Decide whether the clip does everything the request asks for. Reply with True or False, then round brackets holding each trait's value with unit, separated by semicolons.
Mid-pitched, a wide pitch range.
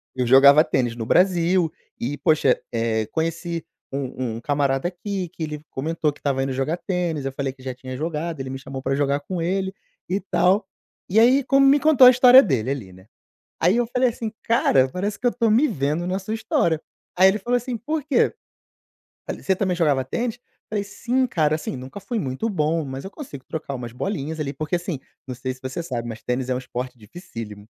True (160 Hz; 7.0 semitones)